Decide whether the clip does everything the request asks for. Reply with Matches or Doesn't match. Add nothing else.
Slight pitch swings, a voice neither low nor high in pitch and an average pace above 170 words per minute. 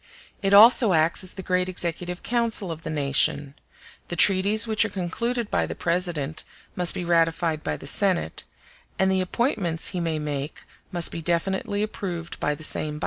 Doesn't match